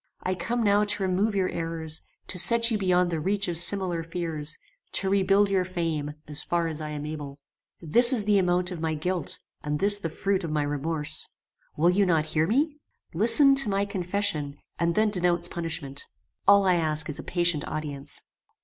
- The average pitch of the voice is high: No, medium, 175 Hz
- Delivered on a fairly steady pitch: No, average, 4.2 semitones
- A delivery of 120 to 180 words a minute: No, average, 195 wpm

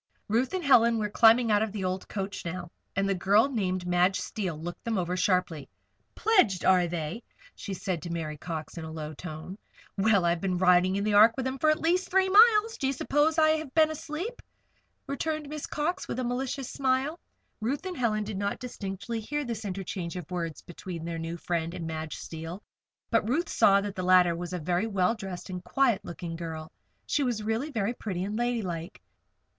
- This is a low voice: No, high, 200 Hz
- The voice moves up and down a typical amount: No, wide, 6.3 semitones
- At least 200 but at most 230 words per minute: Yes, fast, 205 wpm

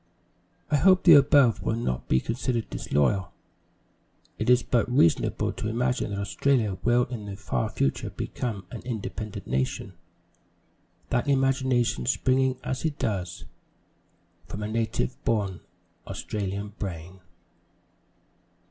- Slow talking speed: Yes, slow, 120 wpm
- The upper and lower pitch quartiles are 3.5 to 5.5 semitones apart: Yes, average, 4.5 semitones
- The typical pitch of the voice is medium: No, low, 115 Hz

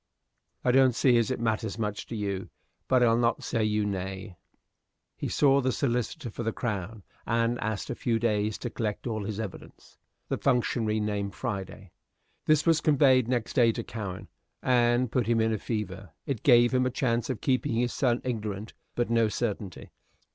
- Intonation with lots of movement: No, average, 2.7 semitones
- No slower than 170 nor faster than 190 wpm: Yes, average, 185 wpm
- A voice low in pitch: Yes, low, 115 Hz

